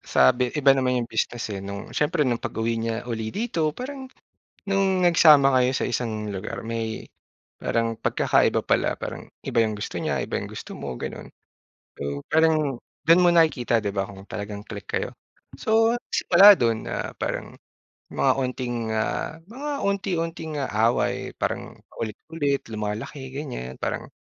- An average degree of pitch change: No, wide, 6.7 semitones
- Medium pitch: No, low, 125 Hz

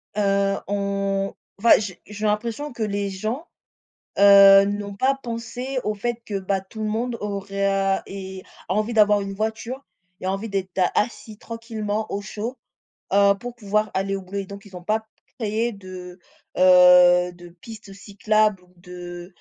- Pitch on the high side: Yes, high, 200 Hz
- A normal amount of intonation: No, narrow, 2.0 semitones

